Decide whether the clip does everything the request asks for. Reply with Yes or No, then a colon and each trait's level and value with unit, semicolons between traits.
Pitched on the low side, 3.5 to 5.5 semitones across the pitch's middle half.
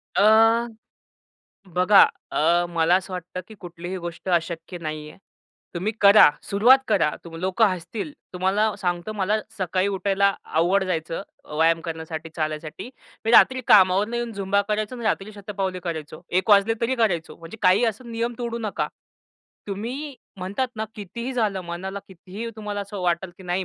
No: high, 195 Hz; average, 3.8 semitones